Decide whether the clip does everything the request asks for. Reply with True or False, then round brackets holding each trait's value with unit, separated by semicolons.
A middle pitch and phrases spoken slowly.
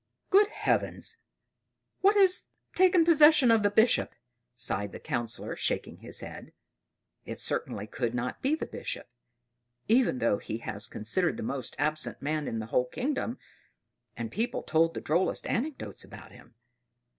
False (175 Hz; 150 wpm)